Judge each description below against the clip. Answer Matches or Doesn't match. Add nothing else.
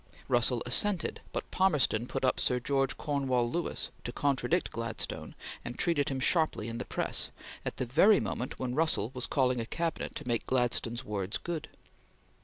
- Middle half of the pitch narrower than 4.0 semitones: Doesn't match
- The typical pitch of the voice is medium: Doesn't match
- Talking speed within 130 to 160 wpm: Doesn't match